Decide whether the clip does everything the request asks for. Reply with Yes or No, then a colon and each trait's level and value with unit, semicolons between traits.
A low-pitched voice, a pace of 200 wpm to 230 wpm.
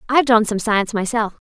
No: high, 220 Hz; fast, 205 wpm